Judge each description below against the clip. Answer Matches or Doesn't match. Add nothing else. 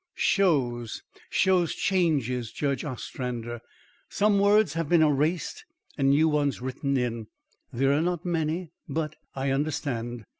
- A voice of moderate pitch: Matches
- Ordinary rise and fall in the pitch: Matches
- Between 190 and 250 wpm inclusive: Doesn't match